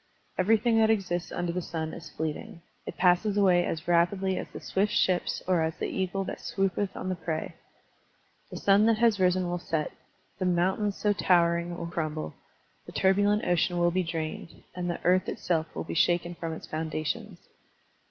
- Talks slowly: No, average, 180 wpm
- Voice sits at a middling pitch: Yes, medium, 175 Hz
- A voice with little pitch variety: Yes, narrow, 2.3 semitones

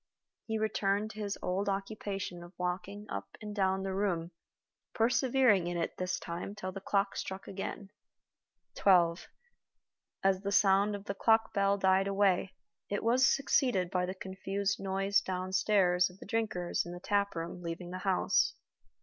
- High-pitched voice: Yes, high, 195 Hz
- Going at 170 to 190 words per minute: No, average, 160 wpm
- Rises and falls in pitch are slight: Yes, narrow, 1.9 semitones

